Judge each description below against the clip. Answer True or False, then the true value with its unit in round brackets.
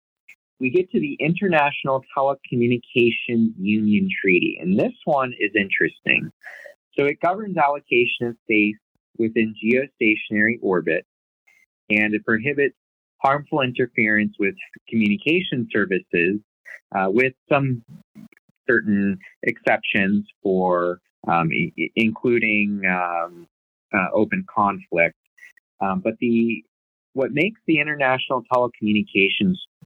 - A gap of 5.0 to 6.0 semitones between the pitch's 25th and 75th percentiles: True (5.5 semitones)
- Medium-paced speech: False (100 wpm)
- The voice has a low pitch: True (115 Hz)